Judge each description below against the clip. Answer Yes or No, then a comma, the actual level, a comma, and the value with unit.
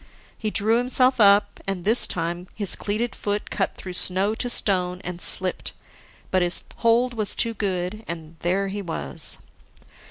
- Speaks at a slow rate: No, average, 160 wpm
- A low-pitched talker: No, high, 200 Hz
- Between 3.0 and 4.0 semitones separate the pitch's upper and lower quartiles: Yes, average, 3.6 semitones